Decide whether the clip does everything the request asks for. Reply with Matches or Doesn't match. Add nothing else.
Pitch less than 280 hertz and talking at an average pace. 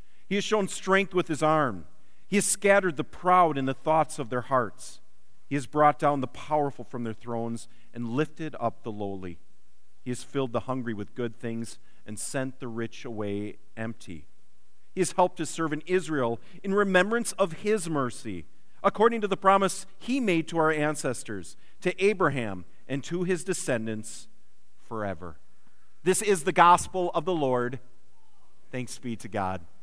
Matches